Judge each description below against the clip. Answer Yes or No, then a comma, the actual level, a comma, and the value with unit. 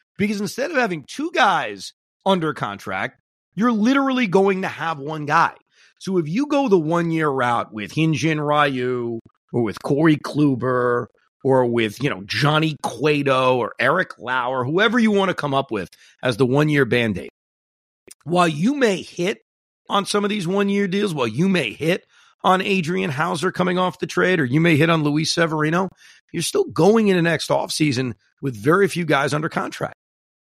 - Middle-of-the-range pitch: Yes, medium, 165 Hz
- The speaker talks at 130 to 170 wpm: No, average, 180 wpm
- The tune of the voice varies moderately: No, wide, 5.9 semitones